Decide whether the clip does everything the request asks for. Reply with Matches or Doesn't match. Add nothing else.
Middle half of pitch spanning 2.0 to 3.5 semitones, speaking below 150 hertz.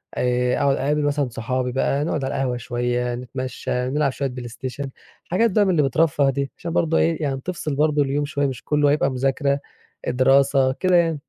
Matches